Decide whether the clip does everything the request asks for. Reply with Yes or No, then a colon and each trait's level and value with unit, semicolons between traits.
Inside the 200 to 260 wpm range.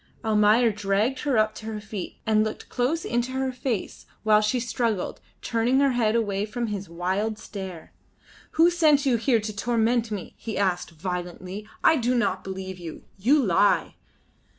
No: average, 170 wpm